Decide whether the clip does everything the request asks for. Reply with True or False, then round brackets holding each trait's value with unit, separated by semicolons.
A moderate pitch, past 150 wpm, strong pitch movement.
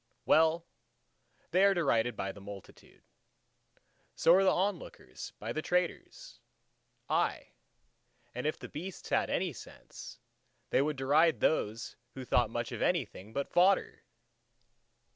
False (155 Hz; 135 wpm; 7.2 semitones)